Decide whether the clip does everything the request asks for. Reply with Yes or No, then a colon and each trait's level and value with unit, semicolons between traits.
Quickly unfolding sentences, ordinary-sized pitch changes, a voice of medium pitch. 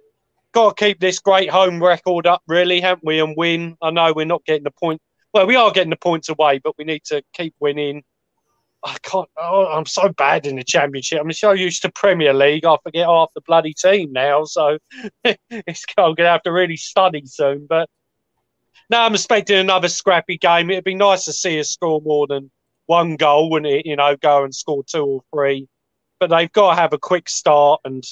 Yes: fast, 215 wpm; average, 3.8 semitones; medium, 170 Hz